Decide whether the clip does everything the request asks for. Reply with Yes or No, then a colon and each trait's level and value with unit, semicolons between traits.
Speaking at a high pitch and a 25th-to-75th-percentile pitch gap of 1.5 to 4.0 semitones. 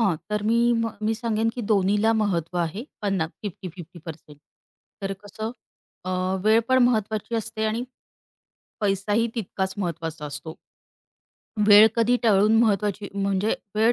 Yes: high, 205 Hz; average, 3.0 semitones